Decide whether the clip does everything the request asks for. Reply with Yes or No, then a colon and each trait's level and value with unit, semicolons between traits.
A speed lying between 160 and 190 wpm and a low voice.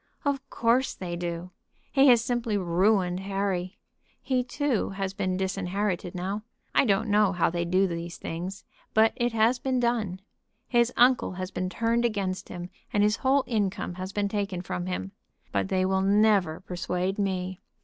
No: average, 170 wpm; high, 195 Hz